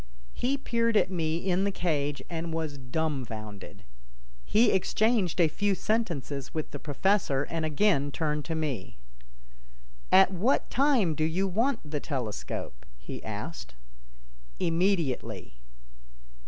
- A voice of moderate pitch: Yes, medium, 165 Hz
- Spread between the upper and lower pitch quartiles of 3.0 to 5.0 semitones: No, wide, 5.5 semitones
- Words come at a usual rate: No, slow, 125 wpm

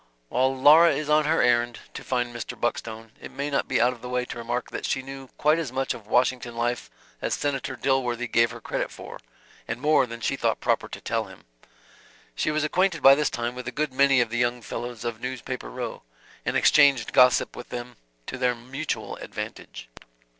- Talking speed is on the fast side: Yes, fast, 210 wpm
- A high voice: No, low, 125 Hz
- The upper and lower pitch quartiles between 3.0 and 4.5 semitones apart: No, narrow, 2.4 semitones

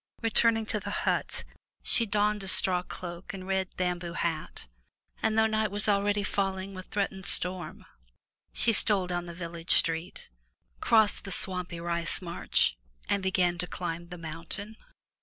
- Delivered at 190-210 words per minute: No, average, 155 wpm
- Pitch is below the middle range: No, medium, 185 Hz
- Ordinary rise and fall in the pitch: Yes, average, 3.0 semitones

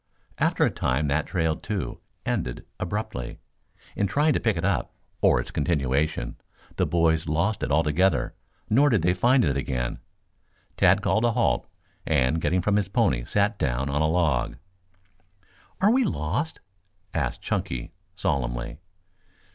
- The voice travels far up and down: Yes, wide, 6.6 semitones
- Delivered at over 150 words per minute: No, average, 145 wpm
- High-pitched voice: No, very low, 80 Hz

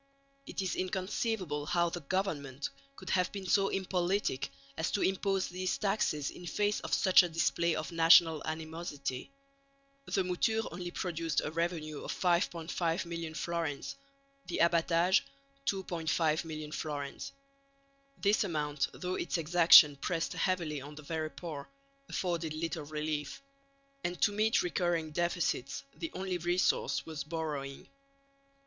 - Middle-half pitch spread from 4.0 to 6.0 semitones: No, average, 2.9 semitones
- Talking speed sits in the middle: No, slow, 130 wpm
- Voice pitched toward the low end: No, medium, 170 Hz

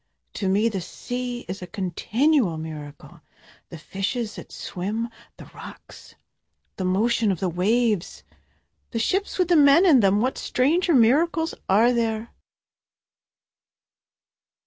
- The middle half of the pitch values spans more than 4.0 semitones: Yes, average, 5.2 semitones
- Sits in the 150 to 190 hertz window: No, high, 225 Hz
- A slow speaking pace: Yes, slow, 125 wpm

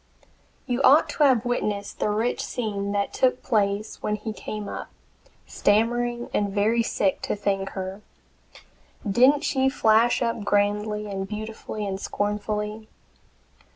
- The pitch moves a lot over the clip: No, average, 2.8 semitones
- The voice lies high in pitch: Yes, high, 210 Hz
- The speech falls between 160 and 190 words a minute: No, slow, 135 wpm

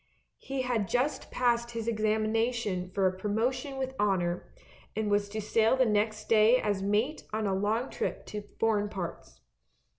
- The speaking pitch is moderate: No, high, 215 Hz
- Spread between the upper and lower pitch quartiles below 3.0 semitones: Yes, narrow, 2.5 semitones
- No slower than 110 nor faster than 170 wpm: Yes, average, 155 wpm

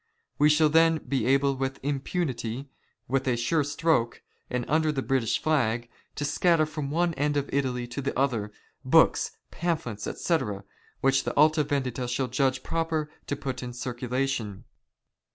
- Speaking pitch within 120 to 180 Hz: Yes, low, 135 Hz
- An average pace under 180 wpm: Yes, average, 170 wpm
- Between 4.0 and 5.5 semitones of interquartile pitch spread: No, average, 3.5 semitones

